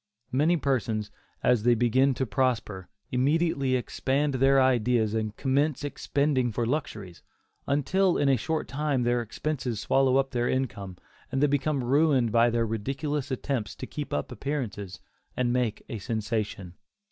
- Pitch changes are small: No, average, 3.7 semitones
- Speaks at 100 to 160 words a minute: Yes, average, 150 wpm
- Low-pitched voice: Yes, low, 130 Hz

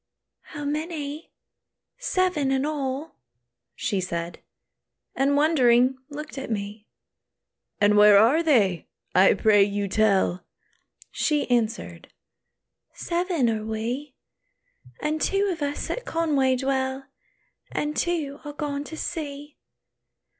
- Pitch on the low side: No, very high, 275 Hz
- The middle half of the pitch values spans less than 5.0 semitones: No, wide, 5.6 semitones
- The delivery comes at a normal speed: No, slow, 110 wpm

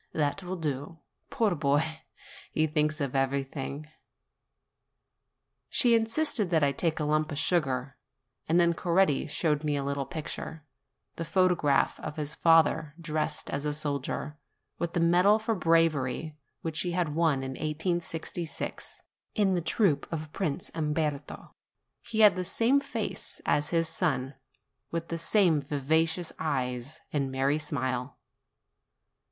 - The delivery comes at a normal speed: Yes, average, 145 wpm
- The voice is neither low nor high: Yes, medium, 155 Hz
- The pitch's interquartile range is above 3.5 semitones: No, average, 3.1 semitones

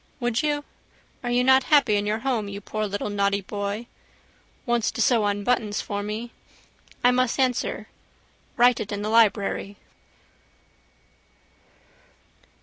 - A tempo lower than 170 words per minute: Yes, average, 140 wpm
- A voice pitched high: Yes, high, 220 Hz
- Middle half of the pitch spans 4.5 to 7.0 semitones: No, average, 3.3 semitones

